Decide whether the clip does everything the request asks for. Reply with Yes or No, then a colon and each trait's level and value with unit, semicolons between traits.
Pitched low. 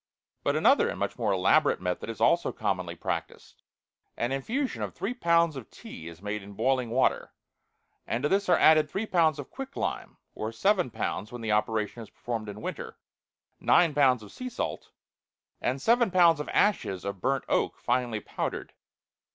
Yes: low, 130 Hz